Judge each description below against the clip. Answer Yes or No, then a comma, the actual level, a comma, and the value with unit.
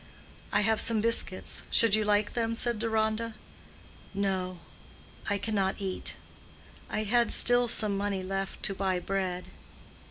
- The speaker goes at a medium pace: No, slow, 130 wpm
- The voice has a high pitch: Yes, high, 205 Hz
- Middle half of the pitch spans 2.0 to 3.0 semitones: Yes, narrow, 2.6 semitones